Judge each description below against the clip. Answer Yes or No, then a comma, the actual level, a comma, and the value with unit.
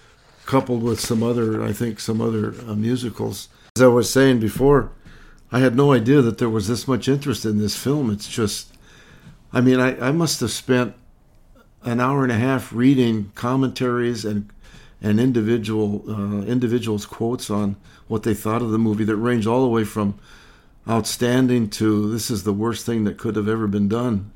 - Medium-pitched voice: No, low, 115 Hz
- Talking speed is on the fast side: No, average, 185 wpm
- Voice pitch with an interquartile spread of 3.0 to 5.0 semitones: No, narrow, 2.6 semitones